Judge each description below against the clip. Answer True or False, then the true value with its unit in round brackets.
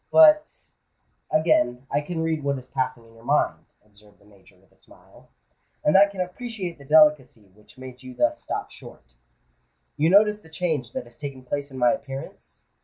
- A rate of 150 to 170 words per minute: False (185 wpm)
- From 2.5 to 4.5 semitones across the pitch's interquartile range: False (5.0 semitones)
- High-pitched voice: False (140 Hz)